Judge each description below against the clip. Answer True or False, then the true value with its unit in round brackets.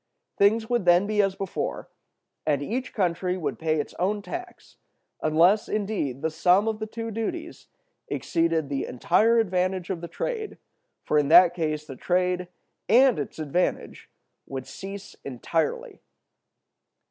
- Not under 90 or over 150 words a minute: True (140 wpm)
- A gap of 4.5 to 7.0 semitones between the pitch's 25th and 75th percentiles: True (5.1 semitones)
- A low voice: False (185 Hz)